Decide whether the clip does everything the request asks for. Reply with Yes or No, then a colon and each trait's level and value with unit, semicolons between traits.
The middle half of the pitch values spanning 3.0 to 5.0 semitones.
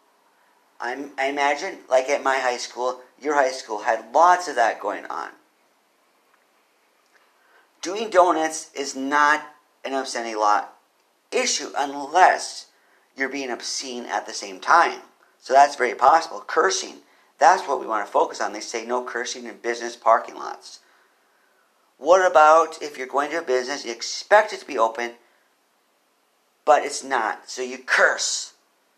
Yes: average, 3.8 semitones